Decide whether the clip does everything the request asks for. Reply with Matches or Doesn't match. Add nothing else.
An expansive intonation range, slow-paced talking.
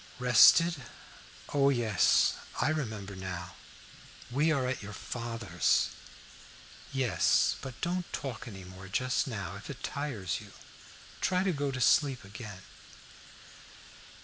Matches